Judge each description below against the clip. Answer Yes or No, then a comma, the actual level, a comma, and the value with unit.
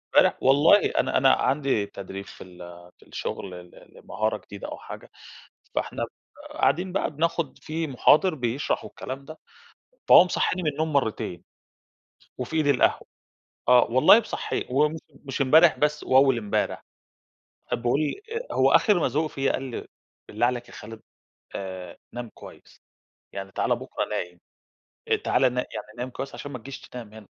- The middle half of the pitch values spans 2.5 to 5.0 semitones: No, wide, 5.6 semitones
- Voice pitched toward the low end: Yes, low, 130 Hz